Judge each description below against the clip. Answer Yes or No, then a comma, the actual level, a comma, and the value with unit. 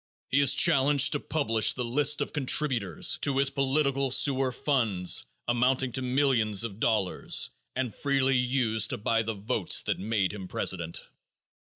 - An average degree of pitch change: Yes, average, 3.7 semitones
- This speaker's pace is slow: No, average, 155 wpm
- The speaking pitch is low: Yes, low, 125 Hz